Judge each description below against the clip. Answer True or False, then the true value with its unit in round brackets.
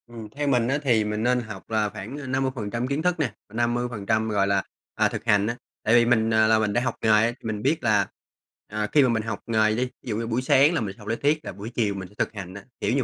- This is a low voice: True (115 Hz)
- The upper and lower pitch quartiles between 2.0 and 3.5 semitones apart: True (2.9 semitones)